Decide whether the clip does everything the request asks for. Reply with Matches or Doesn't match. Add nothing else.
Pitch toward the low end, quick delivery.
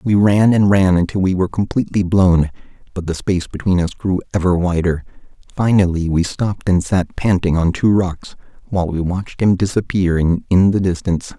Doesn't match